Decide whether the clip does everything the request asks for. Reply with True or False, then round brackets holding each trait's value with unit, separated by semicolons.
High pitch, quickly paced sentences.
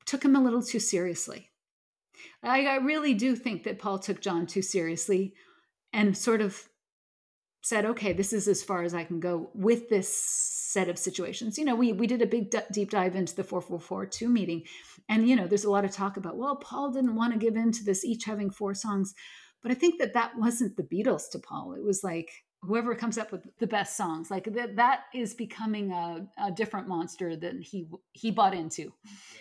True (205 Hz; 220 wpm)